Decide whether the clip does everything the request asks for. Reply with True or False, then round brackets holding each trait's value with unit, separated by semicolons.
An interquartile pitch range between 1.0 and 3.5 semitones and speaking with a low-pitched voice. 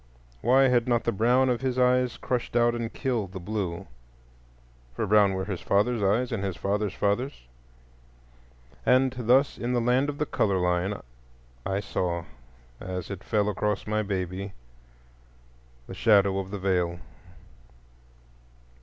False (4.7 semitones; 105 Hz)